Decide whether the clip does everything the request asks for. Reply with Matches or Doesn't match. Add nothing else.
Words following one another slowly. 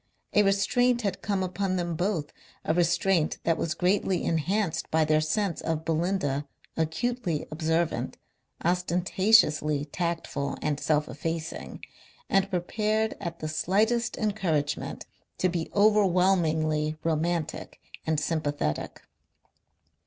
Matches